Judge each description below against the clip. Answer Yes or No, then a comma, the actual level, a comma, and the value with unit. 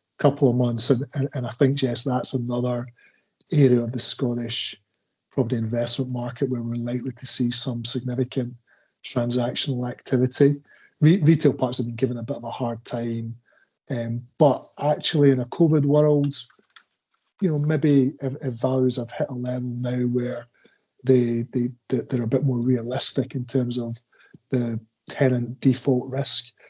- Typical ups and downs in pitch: No, narrow, 2.0 semitones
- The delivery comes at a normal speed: Yes, average, 160 wpm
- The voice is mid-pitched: No, low, 125 Hz